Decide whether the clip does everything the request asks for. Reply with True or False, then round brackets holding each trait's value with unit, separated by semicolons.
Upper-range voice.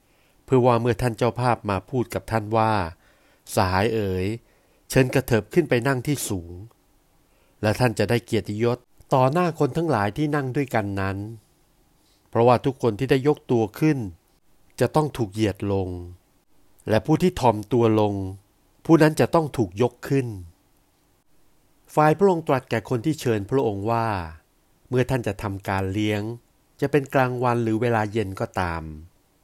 False (115 Hz)